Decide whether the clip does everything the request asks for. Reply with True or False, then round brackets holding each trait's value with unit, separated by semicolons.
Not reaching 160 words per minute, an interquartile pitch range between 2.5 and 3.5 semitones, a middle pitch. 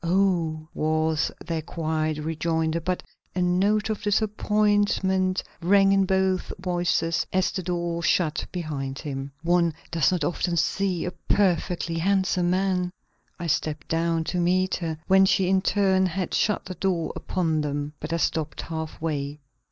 True (150 wpm; 2.9 semitones; 175 Hz)